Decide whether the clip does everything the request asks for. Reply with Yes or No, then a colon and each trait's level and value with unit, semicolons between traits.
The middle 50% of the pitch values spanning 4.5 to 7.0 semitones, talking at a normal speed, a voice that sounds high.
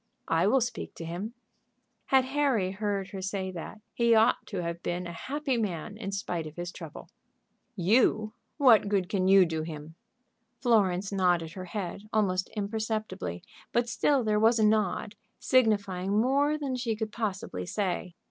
No: average, 3.9 semitones; average, 165 wpm; high, 205 Hz